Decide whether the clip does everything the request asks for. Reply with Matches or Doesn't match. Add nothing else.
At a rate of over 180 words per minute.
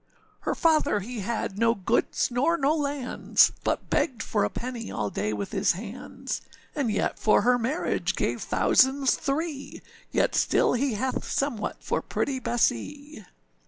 Doesn't match